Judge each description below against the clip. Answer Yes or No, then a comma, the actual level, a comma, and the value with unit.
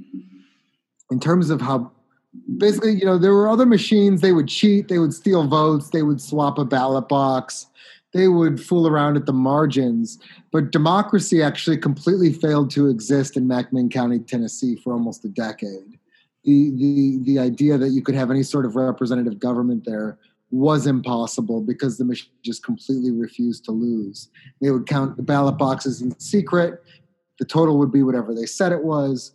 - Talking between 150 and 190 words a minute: Yes, average, 180 wpm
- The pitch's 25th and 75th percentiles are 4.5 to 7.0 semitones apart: Yes, average, 4.8 semitones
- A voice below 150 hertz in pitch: Yes, medium, 140 Hz